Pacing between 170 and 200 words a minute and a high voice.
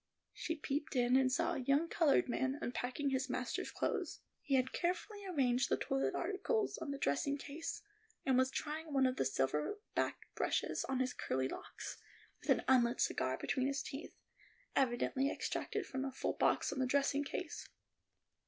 Yes: average, 175 wpm; very high, 270 Hz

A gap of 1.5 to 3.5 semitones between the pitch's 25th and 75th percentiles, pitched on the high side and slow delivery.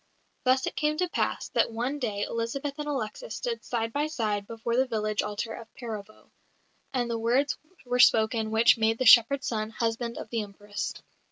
No: average, 3.0 semitones; high, 230 Hz; average, 185 wpm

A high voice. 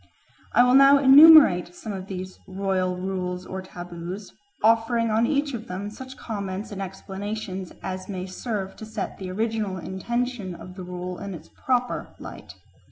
Yes: high, 195 Hz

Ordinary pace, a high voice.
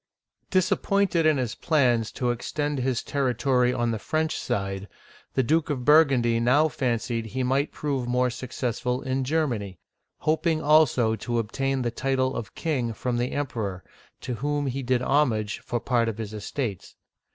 No: average, 160 wpm; low, 125 Hz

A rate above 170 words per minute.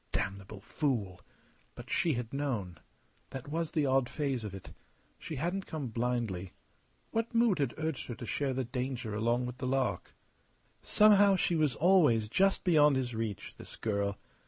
No: average, 165 wpm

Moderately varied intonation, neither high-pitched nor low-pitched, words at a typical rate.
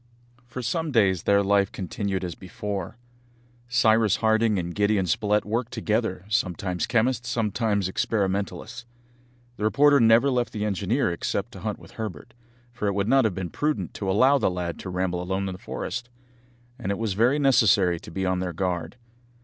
No: average, 3.6 semitones; low, 105 Hz; average, 175 wpm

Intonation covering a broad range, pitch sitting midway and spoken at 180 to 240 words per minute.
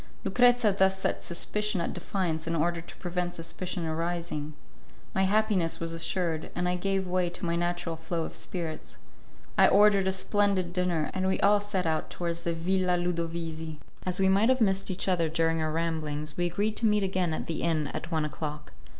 No: narrow, 2.6 semitones; medium, 175 Hz; average, 195 wpm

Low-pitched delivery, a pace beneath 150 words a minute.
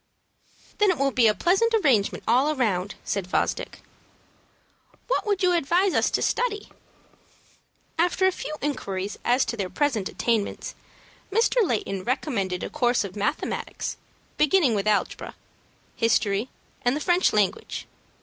No: very high, 255 Hz; average, 140 wpm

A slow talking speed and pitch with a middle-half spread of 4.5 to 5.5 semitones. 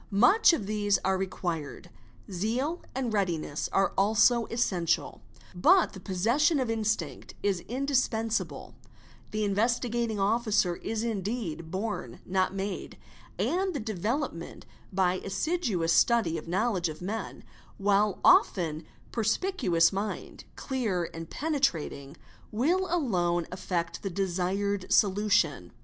Yes: slow, 120 wpm; average, 4.8 semitones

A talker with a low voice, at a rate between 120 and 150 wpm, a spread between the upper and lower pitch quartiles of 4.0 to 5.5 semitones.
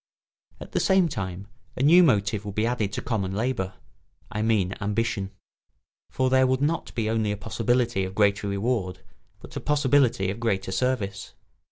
No: low, 110 Hz; average, 170 wpm; average, 4.4 semitones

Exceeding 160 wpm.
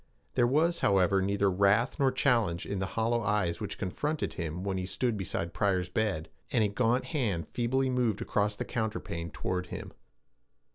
Yes: average, 175 wpm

